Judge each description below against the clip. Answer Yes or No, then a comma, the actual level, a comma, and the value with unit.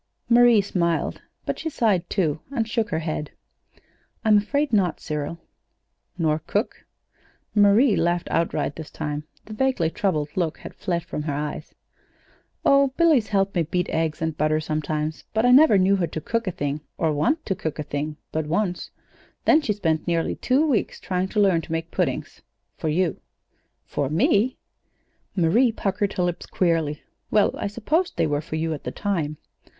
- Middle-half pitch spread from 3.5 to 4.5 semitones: No, wide, 5.4 semitones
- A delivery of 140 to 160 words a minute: No, average, 175 wpm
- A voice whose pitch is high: No, medium, 175 Hz